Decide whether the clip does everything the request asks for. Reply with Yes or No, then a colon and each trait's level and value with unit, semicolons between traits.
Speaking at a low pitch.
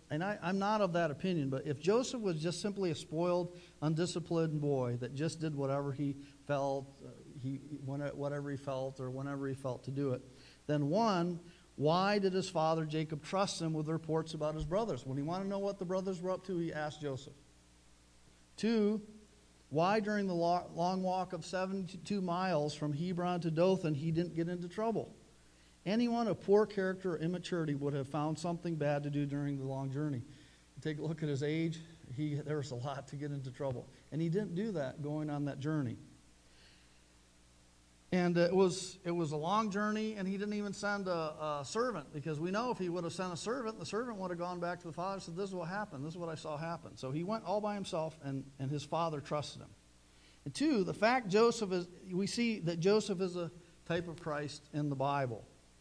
No: medium, 160 Hz